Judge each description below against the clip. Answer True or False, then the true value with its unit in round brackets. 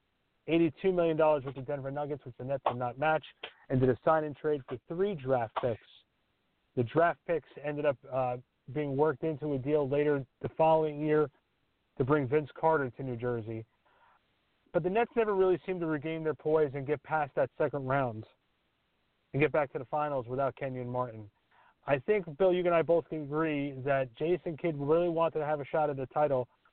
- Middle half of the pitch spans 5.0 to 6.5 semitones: False (3.0 semitones)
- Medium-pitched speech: True (150 Hz)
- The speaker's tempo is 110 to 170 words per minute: False (200 wpm)